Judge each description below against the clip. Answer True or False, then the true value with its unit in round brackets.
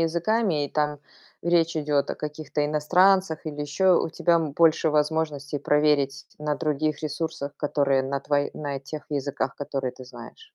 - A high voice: False (150 Hz)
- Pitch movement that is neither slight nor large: False (2.2 semitones)